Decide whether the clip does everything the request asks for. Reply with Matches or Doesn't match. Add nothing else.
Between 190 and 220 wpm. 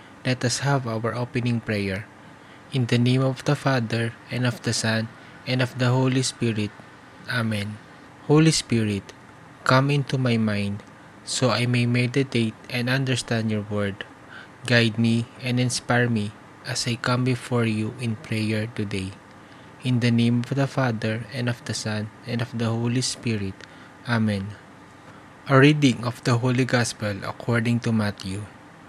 Doesn't match